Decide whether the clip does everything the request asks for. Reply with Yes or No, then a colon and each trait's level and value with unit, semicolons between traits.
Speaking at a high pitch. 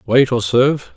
No: low, 125 Hz